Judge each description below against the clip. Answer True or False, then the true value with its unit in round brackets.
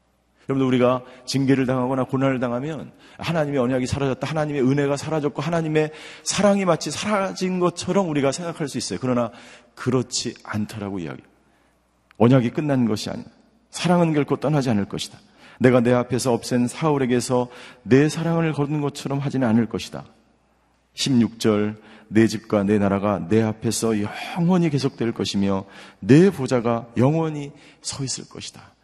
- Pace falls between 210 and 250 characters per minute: False (350 characters per minute)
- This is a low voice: True (130 Hz)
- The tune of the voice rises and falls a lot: False (4.7 semitones)